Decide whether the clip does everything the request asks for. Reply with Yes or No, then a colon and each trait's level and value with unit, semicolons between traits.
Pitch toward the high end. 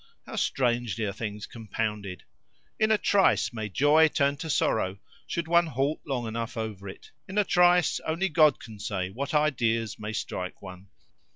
No: low, 120 Hz